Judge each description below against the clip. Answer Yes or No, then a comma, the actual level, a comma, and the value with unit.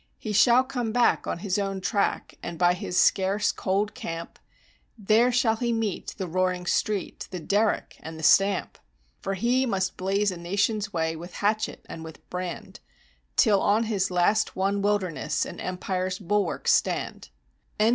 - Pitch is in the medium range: No, high, 195 Hz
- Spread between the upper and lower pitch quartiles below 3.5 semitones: Yes, average, 2.9 semitones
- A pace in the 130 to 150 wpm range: No, average, 160 wpm